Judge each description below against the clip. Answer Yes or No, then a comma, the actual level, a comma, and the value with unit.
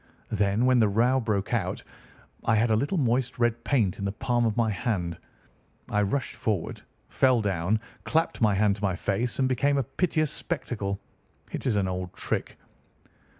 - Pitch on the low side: Yes, low, 110 Hz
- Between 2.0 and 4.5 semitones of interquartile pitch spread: Yes, average, 4.1 semitones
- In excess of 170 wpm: Yes, average, 180 wpm